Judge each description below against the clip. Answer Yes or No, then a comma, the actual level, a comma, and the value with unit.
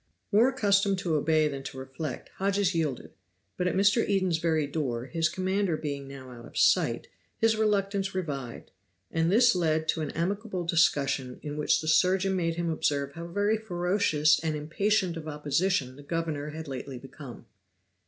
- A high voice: No, medium, 165 Hz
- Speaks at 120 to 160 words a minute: No, average, 170 wpm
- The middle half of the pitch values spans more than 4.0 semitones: Yes, average, 4.8 semitones